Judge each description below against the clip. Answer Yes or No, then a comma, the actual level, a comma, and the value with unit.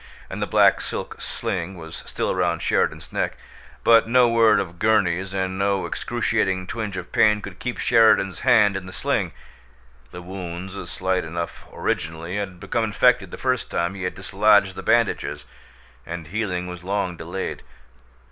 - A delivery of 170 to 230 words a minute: No, average, 160 wpm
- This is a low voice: Yes, very low, 95 Hz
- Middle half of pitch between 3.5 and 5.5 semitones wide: No, average, 3.1 semitones